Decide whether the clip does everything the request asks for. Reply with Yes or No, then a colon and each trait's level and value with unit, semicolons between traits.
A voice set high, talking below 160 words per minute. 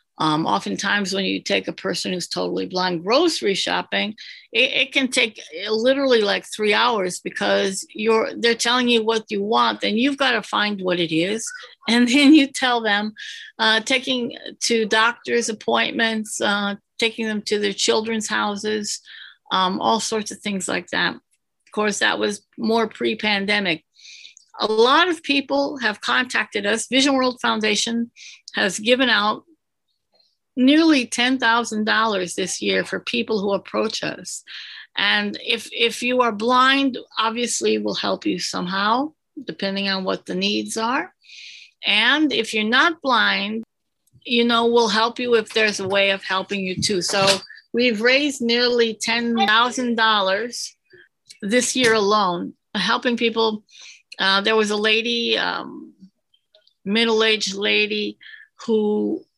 Yes: high, 225 Hz; average, 140 wpm